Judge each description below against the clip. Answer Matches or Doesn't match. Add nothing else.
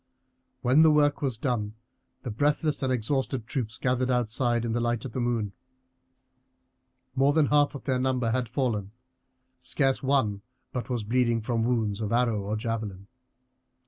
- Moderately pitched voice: Doesn't match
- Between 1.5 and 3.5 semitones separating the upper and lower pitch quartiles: Matches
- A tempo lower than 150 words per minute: Doesn't match